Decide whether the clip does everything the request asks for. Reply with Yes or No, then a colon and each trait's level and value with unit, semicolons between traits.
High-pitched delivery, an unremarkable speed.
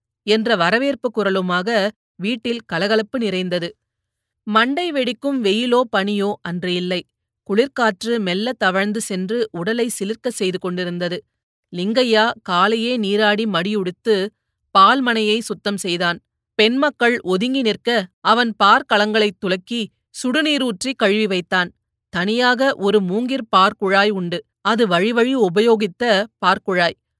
Yes: high, 210 Hz; average, 100 wpm